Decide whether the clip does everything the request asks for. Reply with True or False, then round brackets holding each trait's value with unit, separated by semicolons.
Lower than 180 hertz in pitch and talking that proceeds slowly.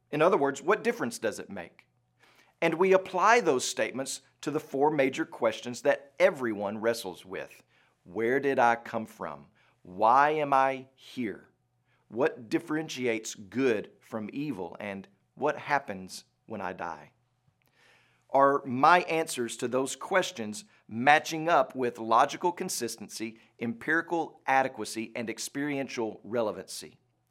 True (135 Hz; 125 wpm)